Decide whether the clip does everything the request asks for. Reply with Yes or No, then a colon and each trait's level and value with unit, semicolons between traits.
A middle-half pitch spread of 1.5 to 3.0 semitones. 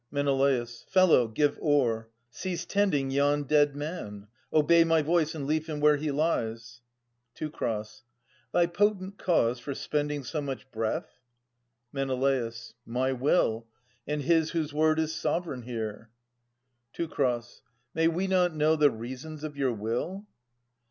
No: average, 4.0 semitones